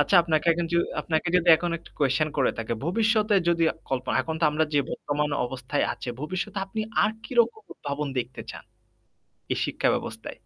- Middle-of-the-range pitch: Yes, medium, 155 Hz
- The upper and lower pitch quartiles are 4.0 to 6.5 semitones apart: Yes, average, 4.6 semitones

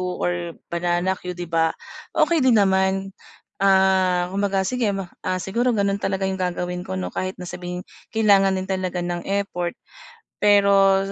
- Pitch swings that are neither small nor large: No, narrow, 1.8 semitones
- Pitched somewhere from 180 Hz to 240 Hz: Yes, high, 190 Hz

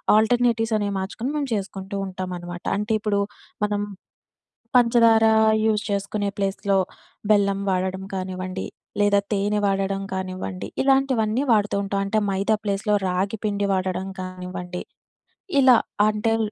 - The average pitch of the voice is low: No, high, 200 Hz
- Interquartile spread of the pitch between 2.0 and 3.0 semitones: Yes, narrow, 2.4 semitones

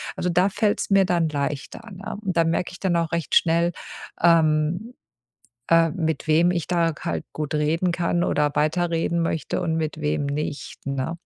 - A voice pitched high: No, medium, 165 Hz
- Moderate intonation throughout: No, narrow, 2.3 semitones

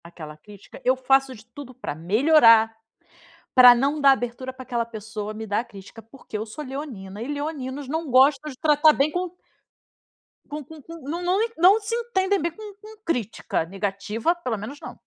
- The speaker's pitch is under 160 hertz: No, very high, 260 Hz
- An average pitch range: No, wide, 5.7 semitones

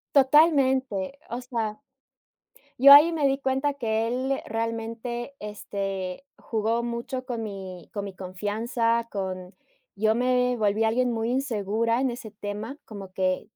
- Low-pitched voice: No, high, 230 Hz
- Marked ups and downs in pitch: No, average, 3.7 semitones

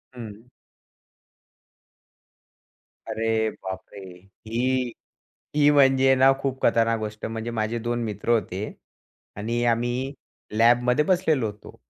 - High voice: No, low, 120 Hz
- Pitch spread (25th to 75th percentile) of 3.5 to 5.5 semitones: No, average, 2.7 semitones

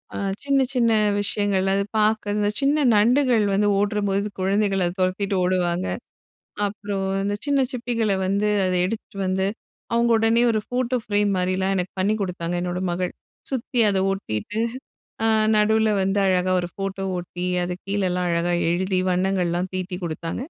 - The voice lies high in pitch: Yes, high, 195 Hz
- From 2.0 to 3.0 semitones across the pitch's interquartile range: Yes, average, 2.7 semitones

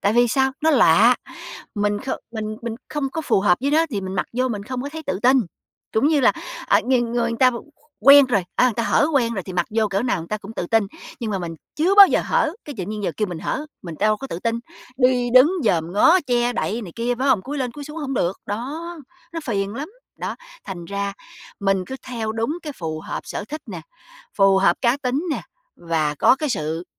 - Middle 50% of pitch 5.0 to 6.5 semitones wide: Yes, average, 5.3 semitones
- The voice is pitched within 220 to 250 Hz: Yes, high, 235 Hz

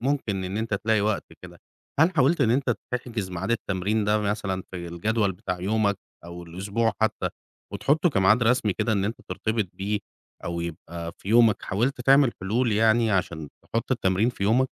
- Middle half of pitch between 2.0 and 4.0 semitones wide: Yes, average, 3.7 semitones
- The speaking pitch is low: Yes, low, 105 Hz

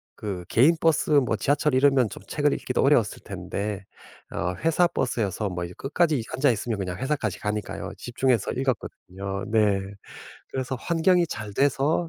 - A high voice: No, low, 125 Hz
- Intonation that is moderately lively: No, wide, 6.0 semitones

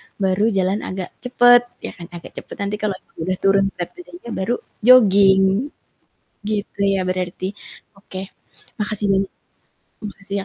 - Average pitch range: No, narrow, 2.0 semitones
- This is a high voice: Yes, high, 195 Hz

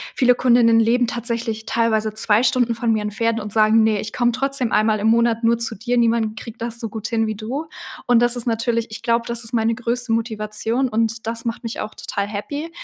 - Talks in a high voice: Yes, high, 230 Hz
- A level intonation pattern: Yes, narrow, 1.4 semitones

